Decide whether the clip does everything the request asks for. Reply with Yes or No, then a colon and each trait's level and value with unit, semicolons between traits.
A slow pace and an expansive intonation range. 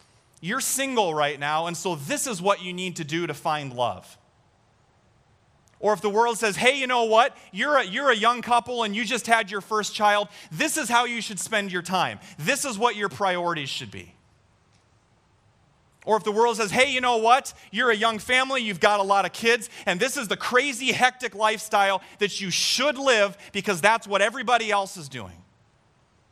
No: fast, 205 wpm; wide, 6.5 semitones